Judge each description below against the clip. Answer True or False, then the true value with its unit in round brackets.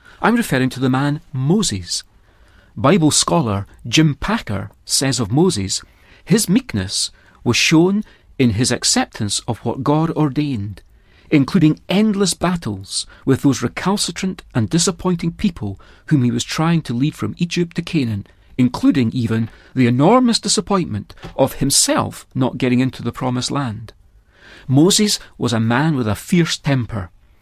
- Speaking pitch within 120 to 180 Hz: True (135 Hz)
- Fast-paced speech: False (140 wpm)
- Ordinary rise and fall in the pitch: False (7.1 semitones)